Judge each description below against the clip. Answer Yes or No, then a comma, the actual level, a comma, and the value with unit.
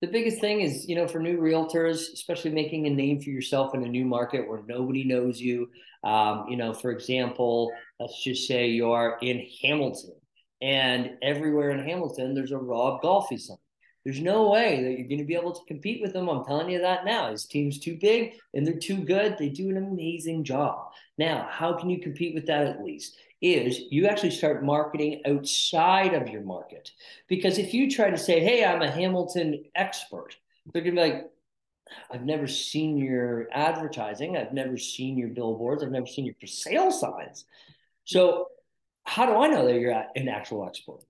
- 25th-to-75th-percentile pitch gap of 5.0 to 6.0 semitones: Yes, average, 5.3 semitones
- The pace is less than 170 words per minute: No, average, 195 wpm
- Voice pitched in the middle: Yes, medium, 145 Hz